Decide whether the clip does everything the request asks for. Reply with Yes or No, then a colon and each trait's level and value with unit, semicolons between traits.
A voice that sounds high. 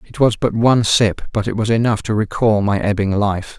No: low, 105 Hz